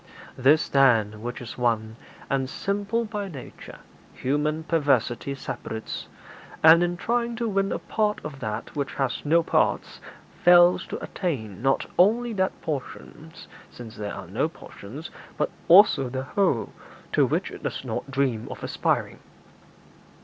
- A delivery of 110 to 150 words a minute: Yes, average, 145 wpm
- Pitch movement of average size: No, wide, 6.7 semitones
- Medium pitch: Yes, medium, 145 Hz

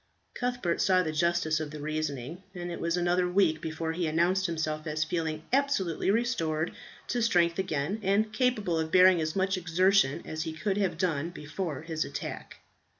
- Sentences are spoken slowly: No, average, 175 wpm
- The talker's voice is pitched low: No, medium, 170 Hz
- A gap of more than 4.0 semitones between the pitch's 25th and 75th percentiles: No, average, 3.3 semitones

